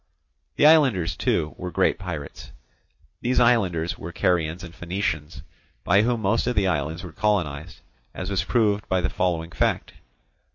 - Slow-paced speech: No, average, 155 wpm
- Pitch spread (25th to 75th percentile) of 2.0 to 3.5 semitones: No, average, 4.2 semitones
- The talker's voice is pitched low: Yes, very low, 90 Hz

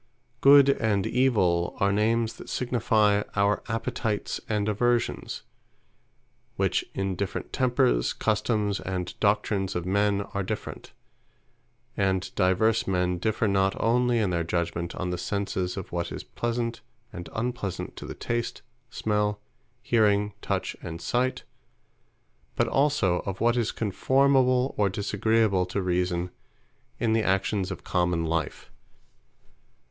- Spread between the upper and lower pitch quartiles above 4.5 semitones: No, average, 3.8 semitones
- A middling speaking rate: No, slow, 130 wpm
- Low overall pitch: Yes, low, 105 Hz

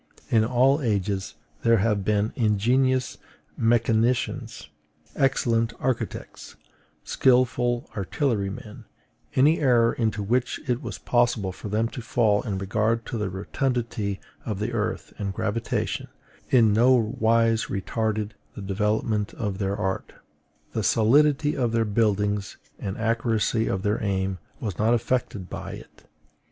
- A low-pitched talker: Yes, low, 110 Hz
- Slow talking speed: Yes, slow, 130 wpm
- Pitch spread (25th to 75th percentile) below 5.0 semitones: Yes, average, 2.8 semitones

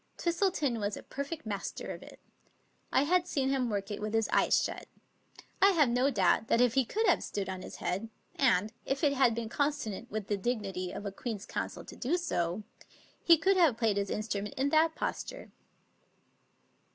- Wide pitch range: Yes, wide, 5.8 semitones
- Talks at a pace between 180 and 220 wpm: Yes, average, 200 wpm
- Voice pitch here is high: Yes, high, 235 Hz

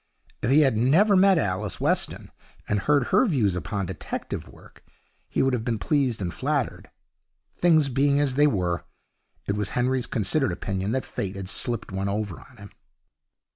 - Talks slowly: No, average, 175 wpm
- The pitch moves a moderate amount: No, wide, 6.1 semitones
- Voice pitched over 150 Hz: No, low, 120 Hz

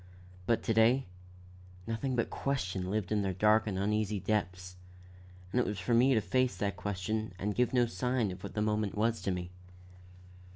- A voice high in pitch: No, low, 105 Hz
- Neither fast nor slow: Yes, average, 190 wpm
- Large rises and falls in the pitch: No, average, 3.4 semitones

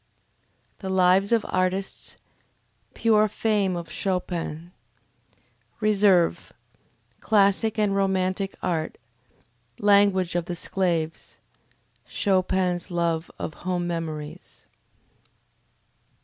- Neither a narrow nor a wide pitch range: No, narrow, 2.3 semitones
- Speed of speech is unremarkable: No, slow, 80 wpm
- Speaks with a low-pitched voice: No, medium, 185 Hz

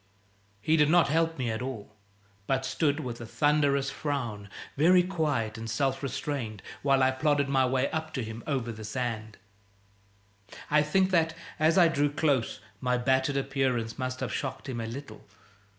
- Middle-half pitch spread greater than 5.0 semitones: No, average, 3.6 semitones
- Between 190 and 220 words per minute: No, average, 170 wpm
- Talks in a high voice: No, low, 135 Hz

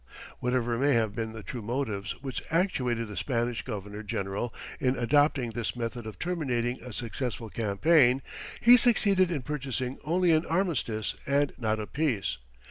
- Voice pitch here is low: Yes, low, 125 Hz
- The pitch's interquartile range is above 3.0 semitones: Yes, average, 4.6 semitones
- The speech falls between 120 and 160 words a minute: Yes, average, 155 wpm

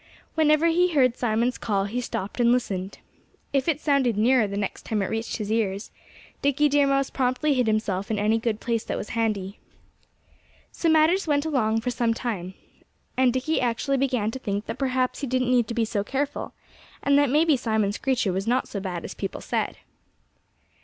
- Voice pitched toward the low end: No, high, 240 Hz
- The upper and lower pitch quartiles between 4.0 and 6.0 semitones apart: Yes, average, 4.3 semitones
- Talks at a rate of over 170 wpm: Yes, average, 195 wpm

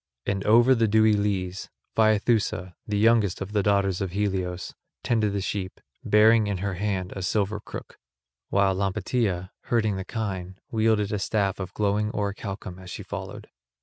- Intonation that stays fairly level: Yes, narrow, 2.2 semitones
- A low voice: Yes, low, 100 Hz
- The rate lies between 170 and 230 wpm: No, average, 160 wpm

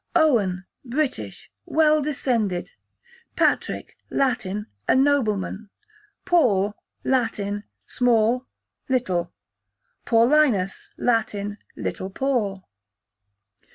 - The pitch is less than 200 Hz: No, high, 225 Hz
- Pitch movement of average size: Yes, average, 4.9 semitones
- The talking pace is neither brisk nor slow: No, slow, 70 wpm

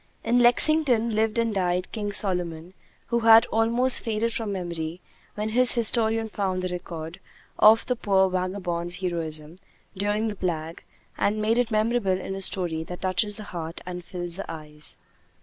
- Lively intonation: No, average, 4.2 semitones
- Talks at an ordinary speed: Yes, average, 165 wpm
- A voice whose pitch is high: Yes, high, 195 Hz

